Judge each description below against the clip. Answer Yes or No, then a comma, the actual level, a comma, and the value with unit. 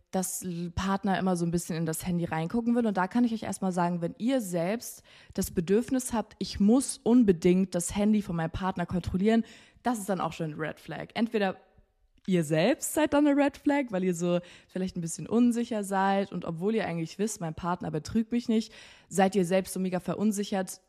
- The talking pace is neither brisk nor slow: No, fast, 210 wpm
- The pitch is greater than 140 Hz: Yes, high, 190 Hz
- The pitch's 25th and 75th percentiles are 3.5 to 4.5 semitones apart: Yes, average, 4.2 semitones